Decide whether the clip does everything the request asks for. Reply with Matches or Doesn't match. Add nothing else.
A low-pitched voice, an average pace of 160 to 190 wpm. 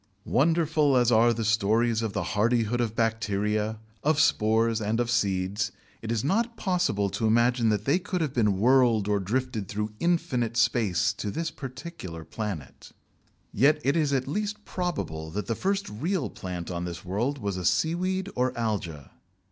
Matches